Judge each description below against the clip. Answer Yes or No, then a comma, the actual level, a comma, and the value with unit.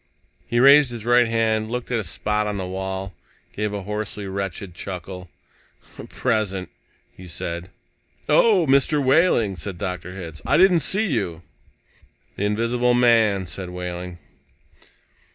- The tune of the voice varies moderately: Yes, average, 4.7 semitones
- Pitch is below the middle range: Yes, low, 105 Hz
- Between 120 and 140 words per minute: Yes, slow, 135 wpm